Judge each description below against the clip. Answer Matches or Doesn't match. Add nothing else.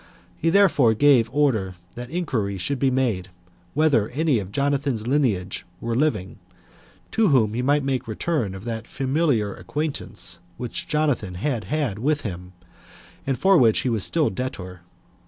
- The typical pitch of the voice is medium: Doesn't match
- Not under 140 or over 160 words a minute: Matches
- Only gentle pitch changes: Doesn't match